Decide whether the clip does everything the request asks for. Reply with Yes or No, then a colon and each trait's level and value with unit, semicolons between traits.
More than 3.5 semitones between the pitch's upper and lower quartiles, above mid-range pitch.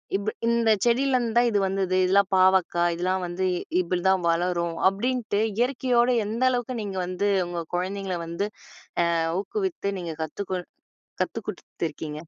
Yes: average, 4.7 semitones; high, 195 Hz